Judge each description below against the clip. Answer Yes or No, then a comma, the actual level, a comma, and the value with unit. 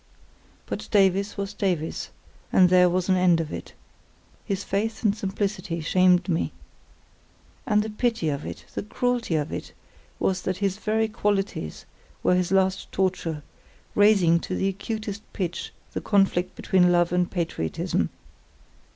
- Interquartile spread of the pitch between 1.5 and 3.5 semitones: Yes, narrow, 2.6 semitones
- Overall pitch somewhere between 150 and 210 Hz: Yes, high, 190 Hz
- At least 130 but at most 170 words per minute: Yes, average, 145 wpm